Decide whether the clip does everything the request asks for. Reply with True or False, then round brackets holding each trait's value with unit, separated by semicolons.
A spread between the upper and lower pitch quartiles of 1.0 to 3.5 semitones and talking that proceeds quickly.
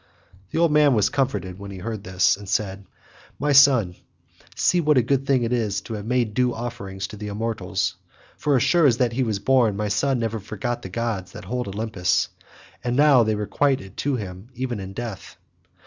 False (4.4 semitones; 210 wpm)